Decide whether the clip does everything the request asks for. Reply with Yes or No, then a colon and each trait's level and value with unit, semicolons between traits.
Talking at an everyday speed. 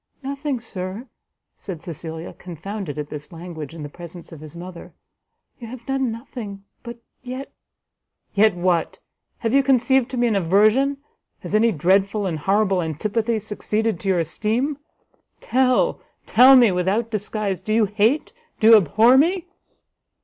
Yes: average, 155 wpm